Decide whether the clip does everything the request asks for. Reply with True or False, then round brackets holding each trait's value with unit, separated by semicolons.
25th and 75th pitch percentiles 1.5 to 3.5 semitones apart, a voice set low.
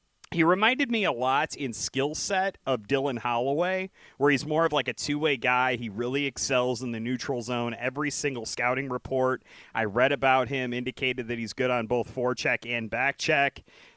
True (3.0 semitones; 130 Hz)